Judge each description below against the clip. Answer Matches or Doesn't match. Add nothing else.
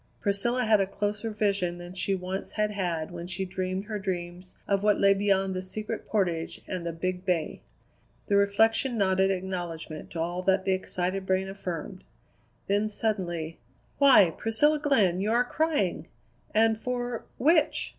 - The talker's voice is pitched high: Matches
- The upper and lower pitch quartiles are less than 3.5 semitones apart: Matches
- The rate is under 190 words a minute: Matches